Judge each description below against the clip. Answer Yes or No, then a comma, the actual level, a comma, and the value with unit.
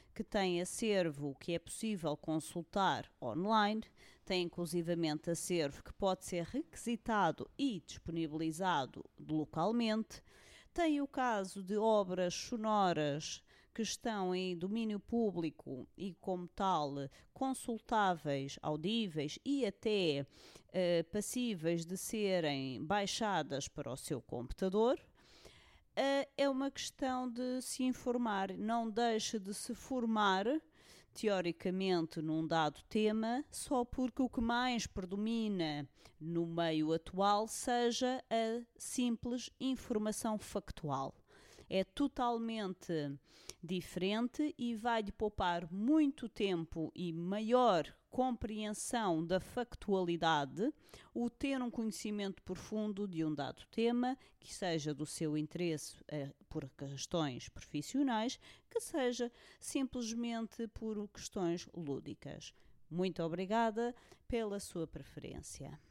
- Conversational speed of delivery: No, slow, 105 wpm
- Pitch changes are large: Yes, wide, 5.9 semitones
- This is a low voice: No, high, 200 Hz